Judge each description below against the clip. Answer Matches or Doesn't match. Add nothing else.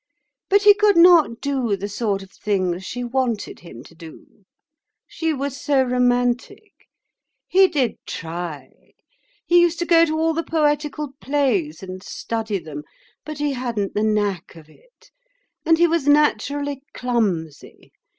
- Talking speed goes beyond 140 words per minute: Matches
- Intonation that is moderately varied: Doesn't match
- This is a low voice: Doesn't match